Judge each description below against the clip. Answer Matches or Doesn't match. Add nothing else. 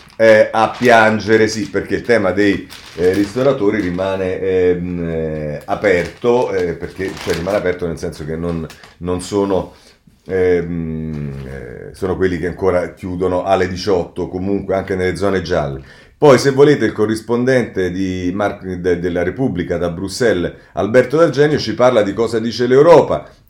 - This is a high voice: Doesn't match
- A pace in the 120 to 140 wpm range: Doesn't match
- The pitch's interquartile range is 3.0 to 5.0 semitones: Matches